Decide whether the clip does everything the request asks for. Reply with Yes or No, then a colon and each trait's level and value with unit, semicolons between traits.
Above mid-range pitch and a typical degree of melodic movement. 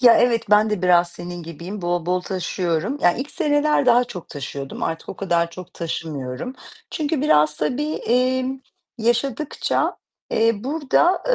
No: high, 210 Hz; wide, 7.1 semitones